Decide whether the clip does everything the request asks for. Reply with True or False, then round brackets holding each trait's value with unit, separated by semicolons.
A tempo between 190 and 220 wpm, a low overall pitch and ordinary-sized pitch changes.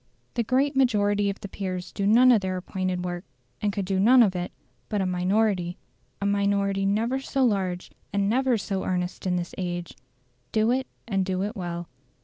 False (195 wpm; 200 Hz; 3.0 semitones)